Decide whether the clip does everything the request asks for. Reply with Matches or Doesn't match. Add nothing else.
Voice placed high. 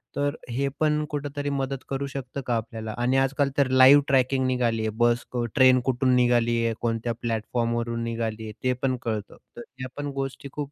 Doesn't match